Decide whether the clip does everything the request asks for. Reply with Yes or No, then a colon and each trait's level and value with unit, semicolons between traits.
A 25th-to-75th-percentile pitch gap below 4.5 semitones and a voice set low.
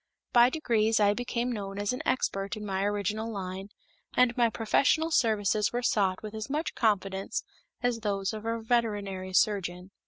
No: average, 3.2 semitones; high, 215 Hz